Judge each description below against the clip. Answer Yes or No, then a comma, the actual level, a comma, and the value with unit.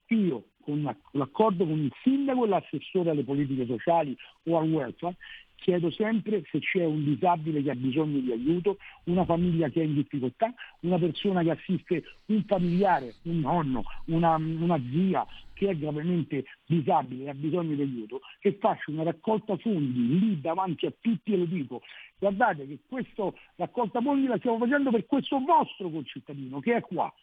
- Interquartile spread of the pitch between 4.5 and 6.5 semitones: Yes, wide, 5.6 semitones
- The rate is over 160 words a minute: Yes, fast, 170 wpm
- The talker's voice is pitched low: No, medium, 170 Hz